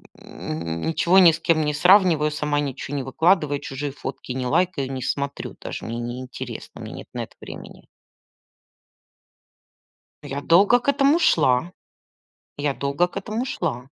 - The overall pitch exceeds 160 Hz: No, medium, 145 Hz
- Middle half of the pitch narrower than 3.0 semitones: No, average, 5.1 semitones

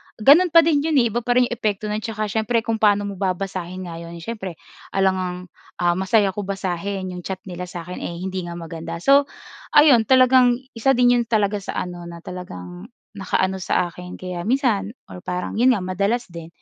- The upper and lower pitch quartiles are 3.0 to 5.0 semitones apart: Yes, average, 4.5 semitones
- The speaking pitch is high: Yes, high, 195 Hz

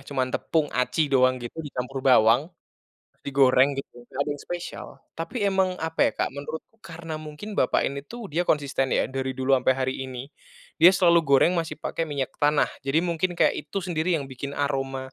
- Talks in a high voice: No, medium, 140 Hz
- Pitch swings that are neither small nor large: Yes, average, 3.8 semitones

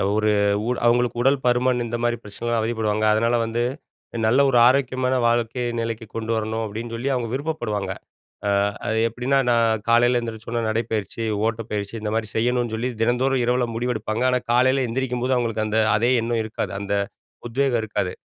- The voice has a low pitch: Yes, low, 115 Hz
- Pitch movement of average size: No, narrow, 1.9 semitones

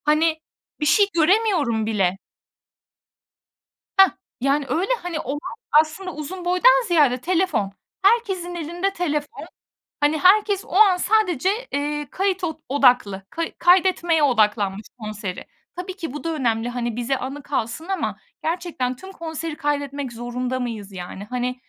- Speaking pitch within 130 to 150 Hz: No, very high, 300 Hz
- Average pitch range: No, wide, 6.5 semitones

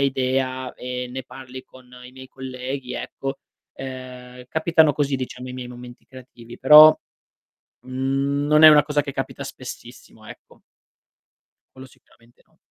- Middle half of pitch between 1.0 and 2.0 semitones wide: Yes, narrow, 1.6 semitones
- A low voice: Yes, low, 130 Hz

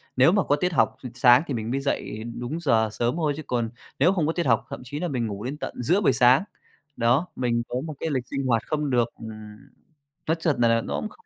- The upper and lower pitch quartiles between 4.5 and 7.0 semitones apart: Yes, average, 4.8 semitones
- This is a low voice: Yes, low, 130 Hz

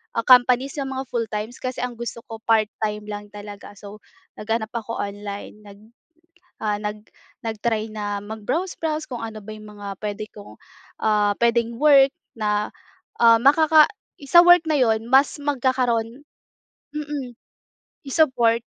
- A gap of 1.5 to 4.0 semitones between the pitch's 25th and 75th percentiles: Yes, average, 3.7 semitones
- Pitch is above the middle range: Yes, high, 225 Hz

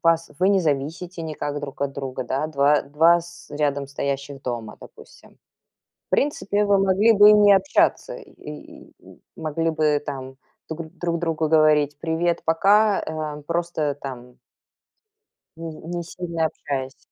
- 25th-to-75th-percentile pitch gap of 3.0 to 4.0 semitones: Yes, average, 3.4 semitones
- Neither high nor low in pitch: Yes, medium, 160 Hz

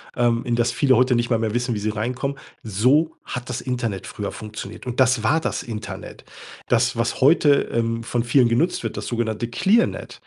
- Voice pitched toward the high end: No, low, 120 Hz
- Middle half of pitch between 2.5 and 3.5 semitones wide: No, narrow, 2.1 semitones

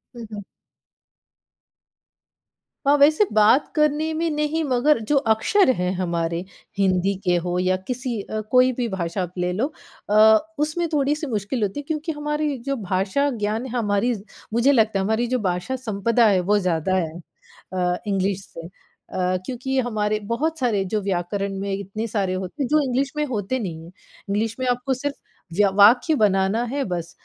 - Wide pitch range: Yes, wide, 6.0 semitones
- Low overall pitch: No, high, 220 Hz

